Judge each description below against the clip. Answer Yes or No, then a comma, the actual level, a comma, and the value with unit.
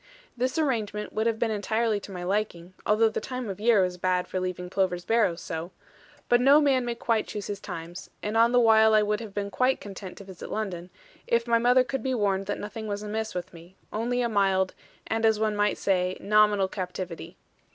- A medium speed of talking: No, fast, 215 wpm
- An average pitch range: Yes, average, 3.4 semitones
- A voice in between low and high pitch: No, high, 210 Hz